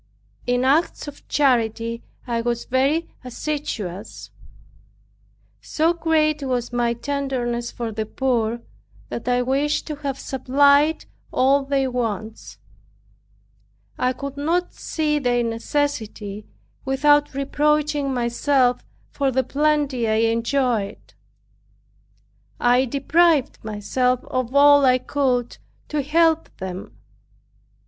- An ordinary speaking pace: No, slow, 105 wpm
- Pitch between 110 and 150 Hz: No, very high, 265 Hz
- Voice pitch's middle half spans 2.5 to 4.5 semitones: Yes, average, 3.4 semitones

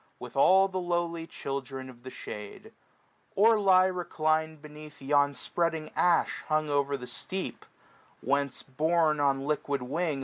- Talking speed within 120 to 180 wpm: Yes, average, 140 wpm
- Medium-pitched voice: Yes, medium, 155 Hz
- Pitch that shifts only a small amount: No, average, 3.7 semitones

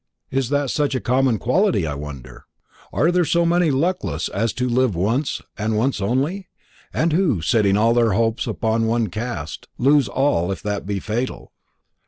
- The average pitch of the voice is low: Yes, low, 120 Hz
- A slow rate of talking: No, average, 175 wpm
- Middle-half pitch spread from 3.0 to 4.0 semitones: No, wide, 5.4 semitones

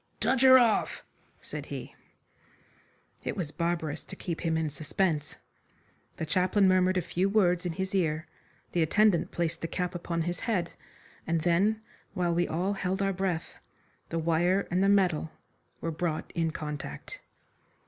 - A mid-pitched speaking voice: Yes, medium, 175 Hz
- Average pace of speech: Yes, average, 160 wpm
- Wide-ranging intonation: No, average, 2.7 semitones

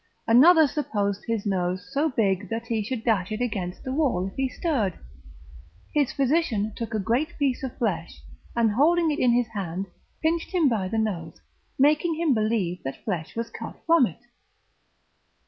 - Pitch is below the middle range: No, high, 230 Hz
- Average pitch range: No, wide, 6.0 semitones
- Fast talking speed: No, average, 175 wpm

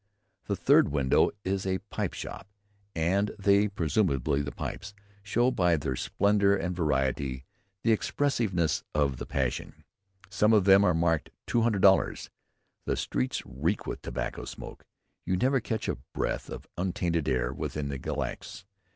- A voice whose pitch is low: Yes, very low, 90 Hz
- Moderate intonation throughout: No, wide, 6.0 semitones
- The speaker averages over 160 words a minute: No, average, 150 wpm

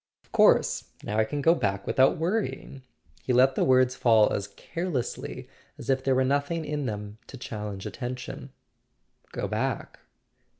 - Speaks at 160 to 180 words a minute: Yes, average, 165 wpm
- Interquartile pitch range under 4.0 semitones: No, average, 4.4 semitones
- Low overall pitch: Yes, low, 130 Hz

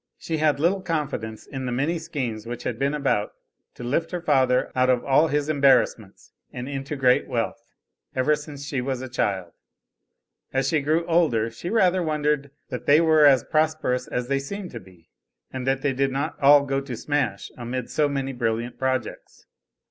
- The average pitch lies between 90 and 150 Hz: Yes, low, 135 Hz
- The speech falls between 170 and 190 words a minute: Yes, average, 185 wpm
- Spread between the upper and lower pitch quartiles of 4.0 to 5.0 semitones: No, average, 3.4 semitones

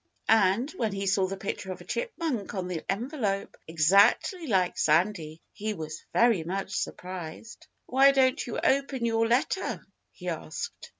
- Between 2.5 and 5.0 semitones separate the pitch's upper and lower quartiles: No, wide, 5.4 semitones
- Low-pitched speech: No, high, 205 Hz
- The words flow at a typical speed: Yes, average, 155 wpm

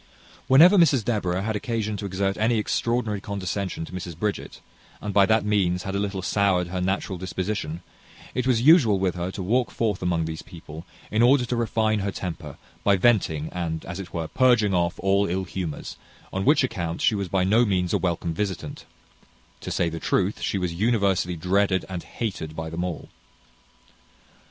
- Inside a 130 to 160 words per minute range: No, average, 185 wpm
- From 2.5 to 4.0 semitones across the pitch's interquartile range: Yes, average, 3.4 semitones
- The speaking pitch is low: Yes, very low, 95 Hz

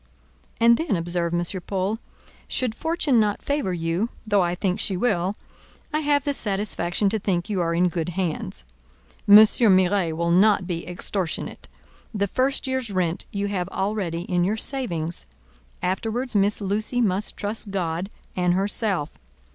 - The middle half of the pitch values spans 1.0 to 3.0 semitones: No, average, 3.7 semitones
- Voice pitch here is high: Yes, high, 195 Hz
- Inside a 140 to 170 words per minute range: Yes, average, 155 wpm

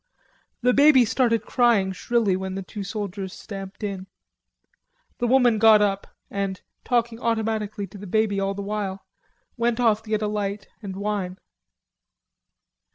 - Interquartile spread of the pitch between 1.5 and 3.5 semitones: Yes, narrow, 2.6 semitones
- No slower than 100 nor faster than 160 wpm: Yes, average, 150 wpm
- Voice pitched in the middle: No, high, 210 Hz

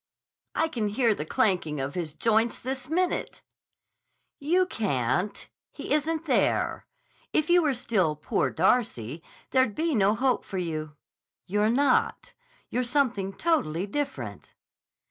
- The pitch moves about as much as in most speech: No, wide, 8.4 semitones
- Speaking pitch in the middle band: No, high, 225 Hz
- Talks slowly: Yes, slow, 130 wpm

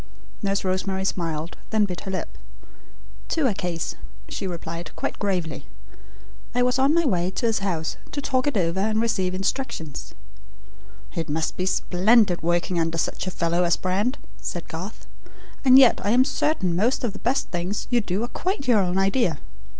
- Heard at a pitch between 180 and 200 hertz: Yes, high, 190 Hz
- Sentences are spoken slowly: No, average, 180 wpm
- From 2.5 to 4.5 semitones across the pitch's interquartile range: No, average, 5.3 semitones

